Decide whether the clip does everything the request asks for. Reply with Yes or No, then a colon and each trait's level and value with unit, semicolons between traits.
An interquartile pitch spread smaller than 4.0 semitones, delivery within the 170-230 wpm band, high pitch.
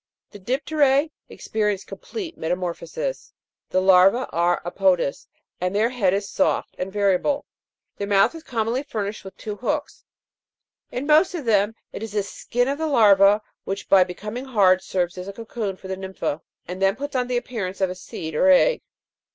No: wide, 5.4 semitones; average, 180 wpm; high, 205 Hz